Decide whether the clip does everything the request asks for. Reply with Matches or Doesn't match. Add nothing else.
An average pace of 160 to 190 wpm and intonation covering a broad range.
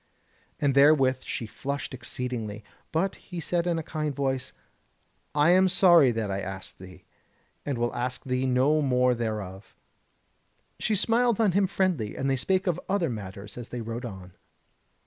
Matches